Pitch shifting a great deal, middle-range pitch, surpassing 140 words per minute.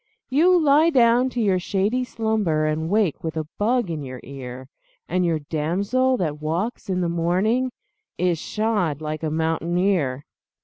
Yes: wide, 6.5 semitones; medium, 180 Hz; average, 160 wpm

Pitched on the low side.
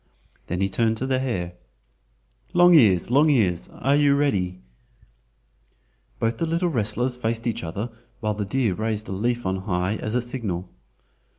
Yes: low, 115 Hz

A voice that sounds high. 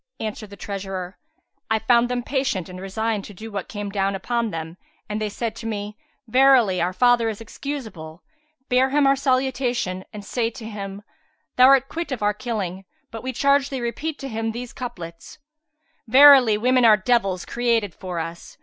Yes: high, 225 Hz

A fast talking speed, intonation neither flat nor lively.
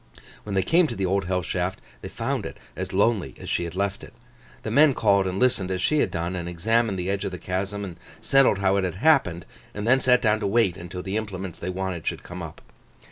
Yes: fast, 245 wpm; average, 3.3 semitones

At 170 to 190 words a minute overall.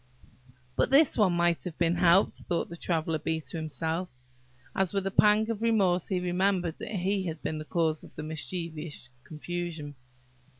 Yes: average, 175 wpm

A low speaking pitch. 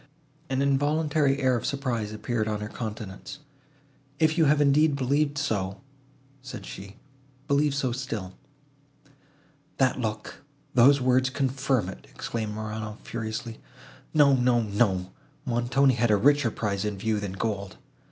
Yes: low, 120 Hz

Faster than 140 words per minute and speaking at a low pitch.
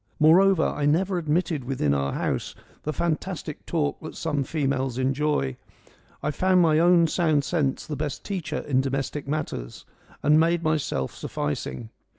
No: average, 150 wpm; medium, 150 Hz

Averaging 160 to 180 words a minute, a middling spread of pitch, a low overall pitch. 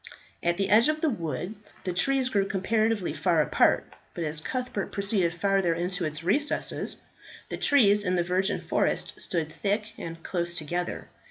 No: average, 165 wpm; average, 3.8 semitones; high, 190 Hz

